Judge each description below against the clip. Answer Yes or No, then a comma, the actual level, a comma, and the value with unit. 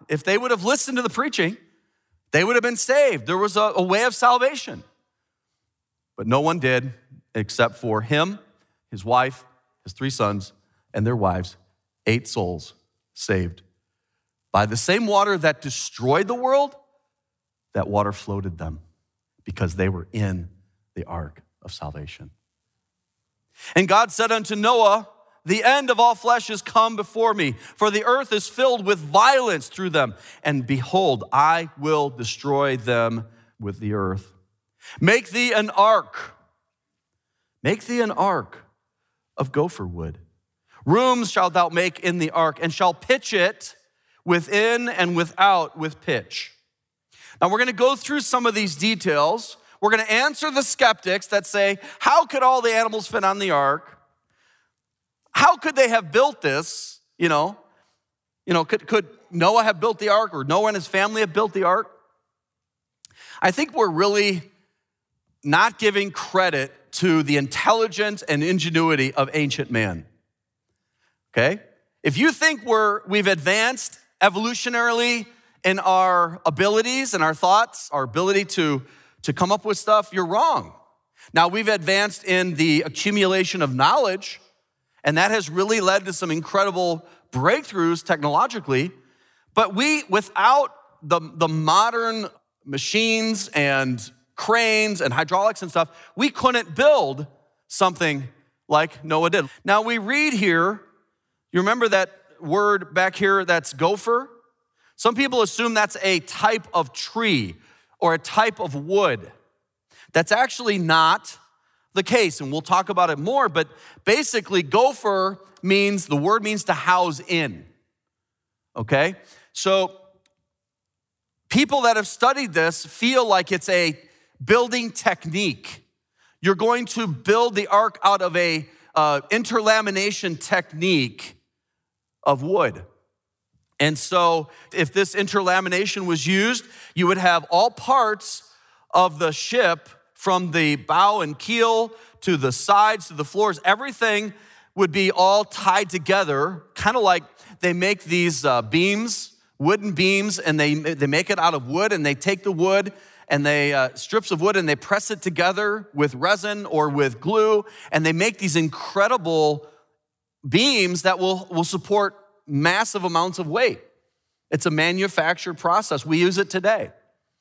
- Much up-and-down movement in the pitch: Yes, wide, 6.3 semitones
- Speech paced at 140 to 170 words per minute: Yes, average, 145 wpm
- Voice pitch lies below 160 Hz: No, medium, 185 Hz